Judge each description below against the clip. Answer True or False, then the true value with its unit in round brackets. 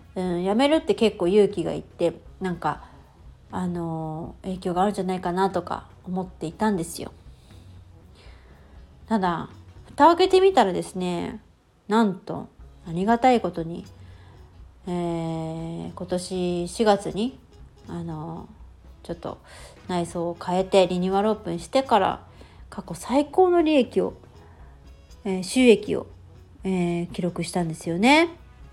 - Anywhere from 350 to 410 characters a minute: False (220 characters per minute)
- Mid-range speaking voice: True (175 Hz)